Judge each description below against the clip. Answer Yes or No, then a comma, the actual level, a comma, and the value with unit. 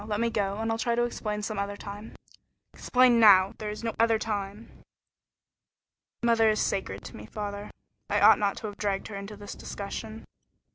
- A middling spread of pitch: No, narrow, 1.9 semitones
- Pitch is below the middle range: No, high, 210 Hz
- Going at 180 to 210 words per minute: Yes, average, 190 wpm